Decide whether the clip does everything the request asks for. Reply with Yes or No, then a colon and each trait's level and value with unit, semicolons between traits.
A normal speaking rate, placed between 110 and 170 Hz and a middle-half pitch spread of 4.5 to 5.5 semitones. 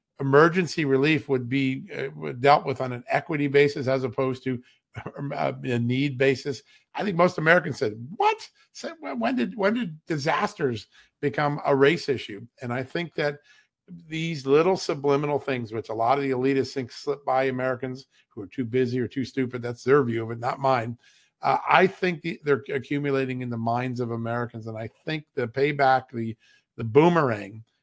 No: average, 175 wpm; low, 135 Hz; average, 2.9 semitones